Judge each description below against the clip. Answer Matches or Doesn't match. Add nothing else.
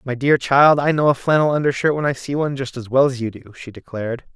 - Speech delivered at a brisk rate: Matches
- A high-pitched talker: Doesn't match